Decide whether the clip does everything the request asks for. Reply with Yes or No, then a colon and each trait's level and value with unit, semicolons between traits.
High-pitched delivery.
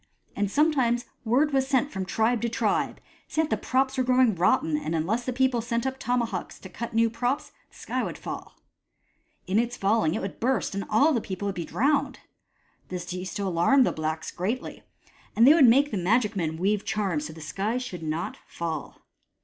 Yes: high, 225 Hz